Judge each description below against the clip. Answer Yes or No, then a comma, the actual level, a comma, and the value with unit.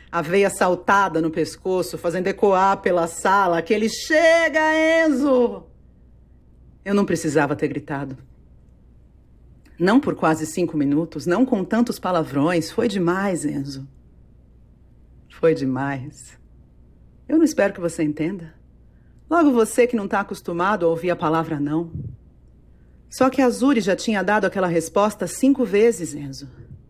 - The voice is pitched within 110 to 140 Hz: No, medium, 170 Hz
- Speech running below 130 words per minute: No, average, 135 wpm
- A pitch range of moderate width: No, wide, 6.9 semitones